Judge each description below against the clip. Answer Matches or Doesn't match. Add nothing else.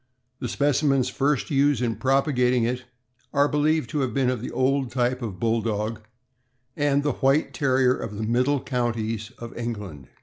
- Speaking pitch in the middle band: Doesn't match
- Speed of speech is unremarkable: Matches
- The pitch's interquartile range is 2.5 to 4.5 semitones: Matches